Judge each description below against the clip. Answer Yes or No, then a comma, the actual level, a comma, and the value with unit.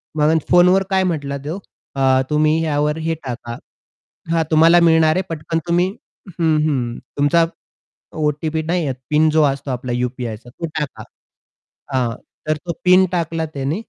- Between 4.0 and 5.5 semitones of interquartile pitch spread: No, average, 3.2 semitones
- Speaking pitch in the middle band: Yes, medium, 155 Hz